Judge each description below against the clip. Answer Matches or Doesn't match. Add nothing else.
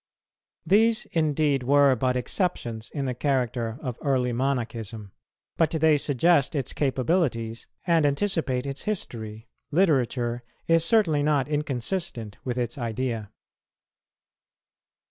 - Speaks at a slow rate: Matches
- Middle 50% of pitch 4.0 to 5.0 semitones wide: Matches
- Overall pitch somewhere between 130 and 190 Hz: Matches